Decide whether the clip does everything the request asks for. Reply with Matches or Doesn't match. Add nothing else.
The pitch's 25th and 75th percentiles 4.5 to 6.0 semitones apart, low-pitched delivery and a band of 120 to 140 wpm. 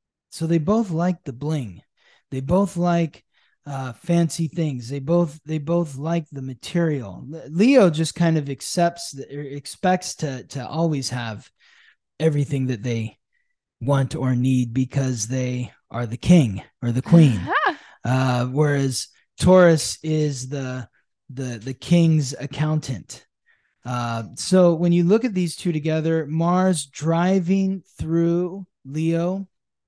Doesn't match